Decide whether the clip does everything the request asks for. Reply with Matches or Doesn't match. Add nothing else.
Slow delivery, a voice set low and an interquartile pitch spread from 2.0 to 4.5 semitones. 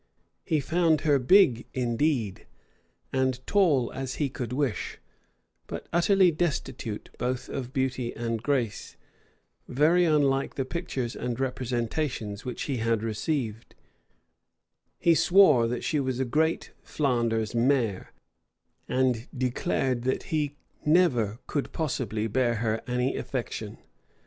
Matches